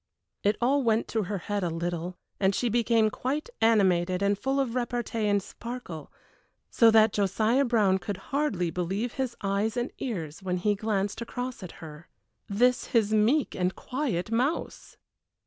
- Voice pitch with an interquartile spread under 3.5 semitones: No, average, 4.2 semitones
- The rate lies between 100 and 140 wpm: No, average, 165 wpm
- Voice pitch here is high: Yes, high, 215 Hz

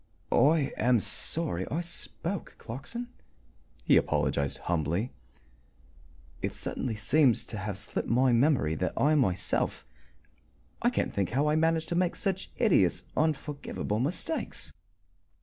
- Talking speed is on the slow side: Yes, slow, 125 wpm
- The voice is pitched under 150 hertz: Yes, low, 135 Hz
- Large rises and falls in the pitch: Yes, wide, 7.7 semitones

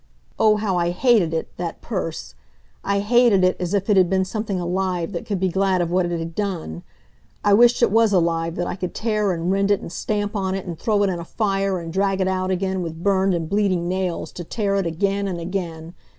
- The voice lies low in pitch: No, high, 190 Hz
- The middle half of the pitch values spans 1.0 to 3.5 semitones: Yes, narrow, 2.5 semitones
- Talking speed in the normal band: No, fast, 235 wpm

